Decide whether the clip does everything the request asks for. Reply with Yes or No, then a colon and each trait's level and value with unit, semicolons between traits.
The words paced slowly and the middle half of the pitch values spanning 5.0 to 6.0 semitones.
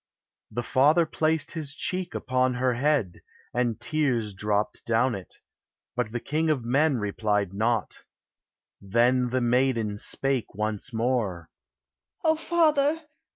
Yes: slow, 125 wpm; average, 5.3 semitones